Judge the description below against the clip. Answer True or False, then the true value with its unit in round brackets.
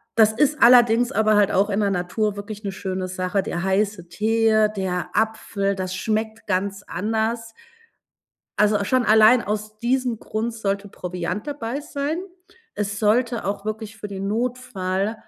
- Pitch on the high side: True (215 Hz)